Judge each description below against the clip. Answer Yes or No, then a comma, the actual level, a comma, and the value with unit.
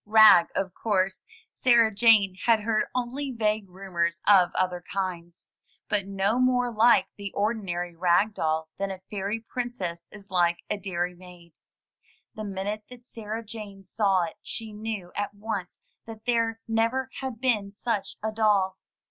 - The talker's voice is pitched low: No, high, 205 Hz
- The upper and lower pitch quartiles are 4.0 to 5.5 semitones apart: No, average, 3.3 semitones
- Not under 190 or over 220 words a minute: No, average, 155 wpm